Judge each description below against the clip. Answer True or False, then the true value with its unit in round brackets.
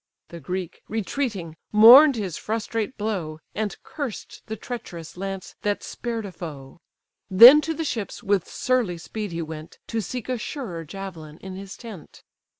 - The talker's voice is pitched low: False (200 Hz)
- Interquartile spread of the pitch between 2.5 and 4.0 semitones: False (5.1 semitones)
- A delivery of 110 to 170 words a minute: True (155 wpm)